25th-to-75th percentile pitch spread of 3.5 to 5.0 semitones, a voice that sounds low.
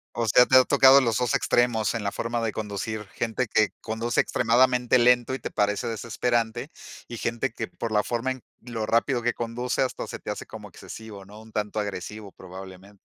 No: narrow, 2.5 semitones; low, 115 Hz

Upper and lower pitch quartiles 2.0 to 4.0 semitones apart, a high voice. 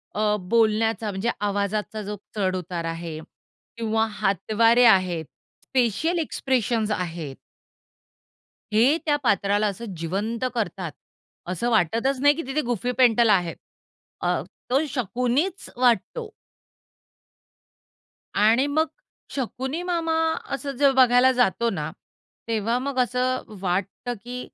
No: average, 4.4 semitones; high, 230 Hz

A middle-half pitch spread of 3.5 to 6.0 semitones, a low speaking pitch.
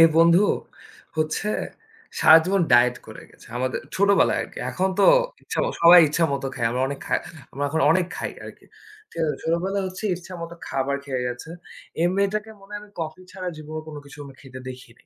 No: average, 5.0 semitones; medium, 160 Hz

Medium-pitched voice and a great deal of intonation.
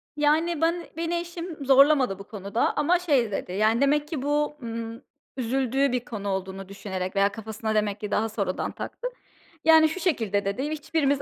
No: very high, 255 Hz; wide, 6.4 semitones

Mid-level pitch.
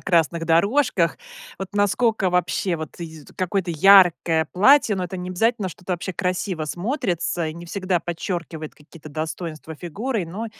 Yes: medium, 180 Hz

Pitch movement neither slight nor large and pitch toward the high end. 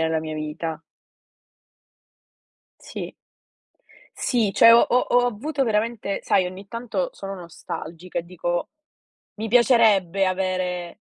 Yes: average, 4.9 semitones; high, 195 Hz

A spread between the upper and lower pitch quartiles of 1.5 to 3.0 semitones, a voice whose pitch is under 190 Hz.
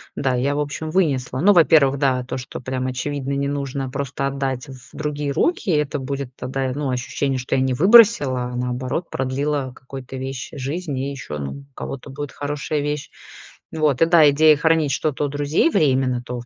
Yes: narrow, 2.4 semitones; medium, 140 Hz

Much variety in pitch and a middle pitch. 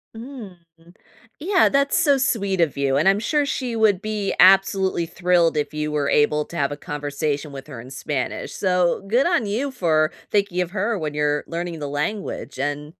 Yes: wide, 6.2 semitones; medium, 175 Hz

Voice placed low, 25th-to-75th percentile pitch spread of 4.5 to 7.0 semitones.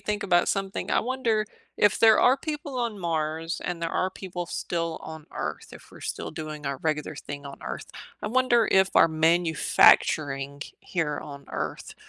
No: medium, 170 Hz; wide, 5.4 semitones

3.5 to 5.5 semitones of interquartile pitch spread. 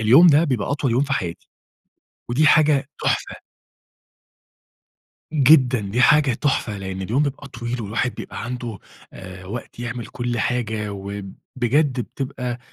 Yes: average, 4.4 semitones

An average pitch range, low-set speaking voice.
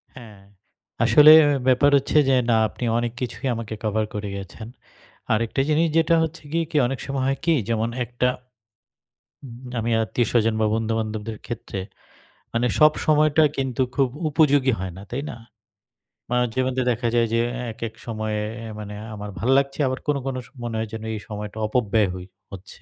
Yes: average, 3.7 semitones; low, 120 Hz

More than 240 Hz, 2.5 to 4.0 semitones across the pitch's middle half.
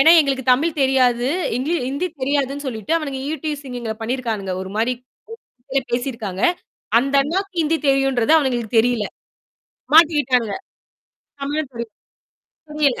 Yes: very high, 265 Hz; average, 3.5 semitones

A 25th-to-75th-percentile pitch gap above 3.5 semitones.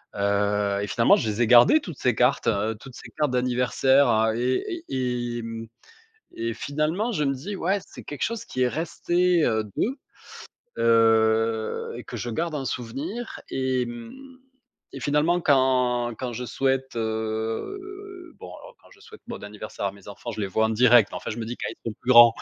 Yes: average, 5.3 semitones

